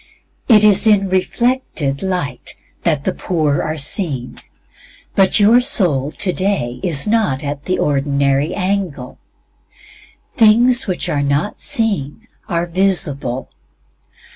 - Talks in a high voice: No, medium, 175 Hz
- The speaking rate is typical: No, slow, 115 wpm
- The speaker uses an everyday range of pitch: No, wide, 6.3 semitones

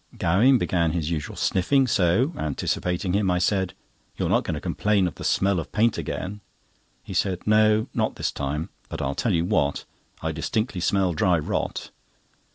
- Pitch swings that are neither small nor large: Yes, average, 4.2 semitones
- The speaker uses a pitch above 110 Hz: No, very low, 90 Hz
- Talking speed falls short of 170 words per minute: No, average, 175 wpm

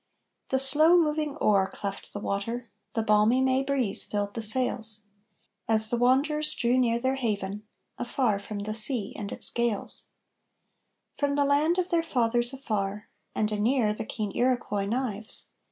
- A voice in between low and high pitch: No, high, 235 Hz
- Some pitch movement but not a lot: Yes, average, 4.2 semitones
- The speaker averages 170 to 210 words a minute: No, average, 155 wpm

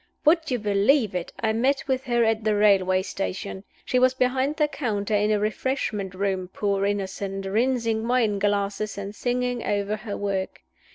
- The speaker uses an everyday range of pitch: Yes, average, 3.9 semitones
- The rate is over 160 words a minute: Yes, average, 170 wpm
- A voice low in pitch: No, high, 210 Hz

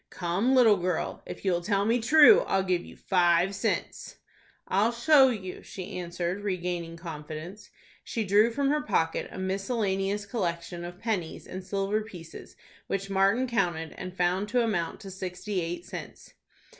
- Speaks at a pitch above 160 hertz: Yes, high, 190 Hz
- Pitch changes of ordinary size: Yes, average, 3.4 semitones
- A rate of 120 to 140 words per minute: No, average, 155 wpm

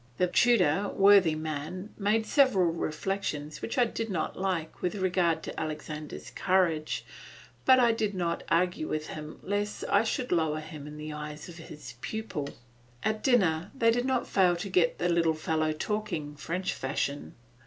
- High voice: No, medium, 175 Hz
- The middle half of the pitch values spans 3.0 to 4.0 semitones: No, average, 4.8 semitones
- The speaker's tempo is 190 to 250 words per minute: No, average, 165 wpm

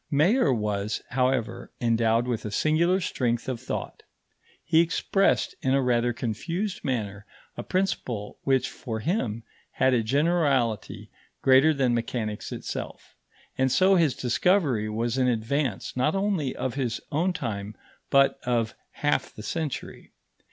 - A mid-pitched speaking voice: No, low, 130 Hz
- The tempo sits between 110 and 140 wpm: Yes, slow, 135 wpm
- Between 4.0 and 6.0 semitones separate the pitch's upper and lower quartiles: Yes, average, 5.3 semitones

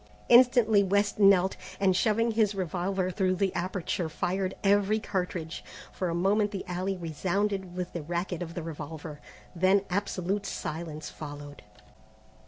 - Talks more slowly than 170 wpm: Yes, average, 140 wpm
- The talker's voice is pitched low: No, medium, 185 Hz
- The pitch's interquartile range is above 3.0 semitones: No, average, 2.7 semitones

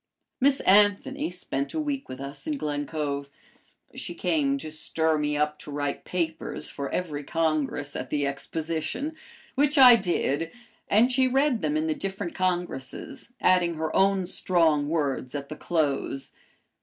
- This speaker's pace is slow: No, average, 155 wpm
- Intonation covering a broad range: Yes, wide, 5.9 semitones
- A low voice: No, medium, 165 Hz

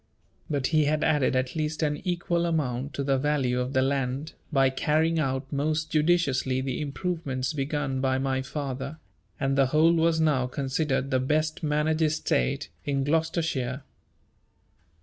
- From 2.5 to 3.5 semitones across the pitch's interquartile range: Yes, average, 2.9 semitones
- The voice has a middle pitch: Yes, medium, 145 Hz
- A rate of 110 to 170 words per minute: Yes, average, 150 wpm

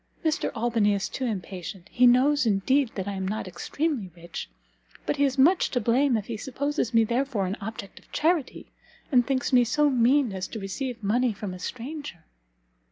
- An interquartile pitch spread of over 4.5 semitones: Yes, average, 5.3 semitones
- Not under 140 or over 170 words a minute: No, average, 190 wpm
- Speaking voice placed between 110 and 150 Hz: No, high, 240 Hz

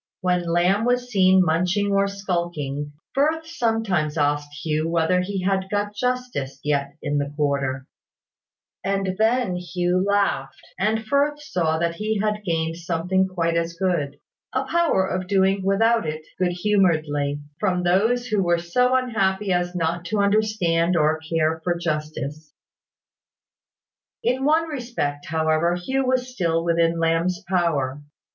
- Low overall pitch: No, medium, 180 Hz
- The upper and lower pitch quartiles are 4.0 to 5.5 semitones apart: Yes, average, 4.5 semitones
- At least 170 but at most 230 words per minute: No, average, 140 wpm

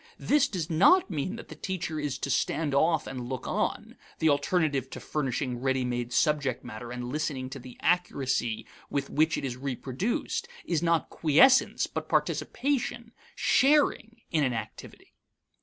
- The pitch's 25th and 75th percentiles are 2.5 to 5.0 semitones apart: No, wide, 5.4 semitones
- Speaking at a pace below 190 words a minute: Yes, average, 155 wpm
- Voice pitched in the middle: Yes, medium, 150 Hz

